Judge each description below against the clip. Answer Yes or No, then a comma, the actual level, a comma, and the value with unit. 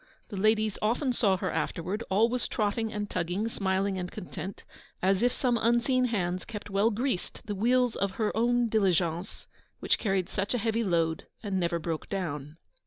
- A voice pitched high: Yes, high, 205 Hz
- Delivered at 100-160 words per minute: No, average, 175 wpm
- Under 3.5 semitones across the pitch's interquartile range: No, average, 3.9 semitones